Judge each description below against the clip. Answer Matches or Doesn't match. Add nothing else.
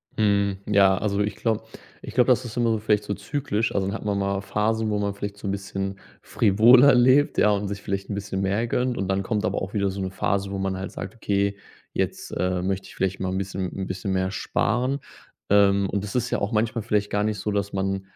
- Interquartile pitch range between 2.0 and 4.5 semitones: Doesn't match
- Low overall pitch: Matches